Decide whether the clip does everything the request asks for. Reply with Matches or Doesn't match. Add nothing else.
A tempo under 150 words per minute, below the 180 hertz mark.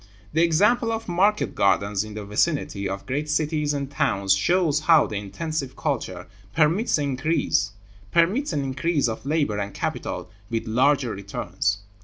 Matches